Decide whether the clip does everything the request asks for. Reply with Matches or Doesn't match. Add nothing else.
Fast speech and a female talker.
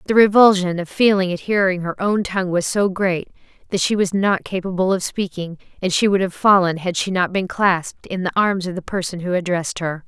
Matches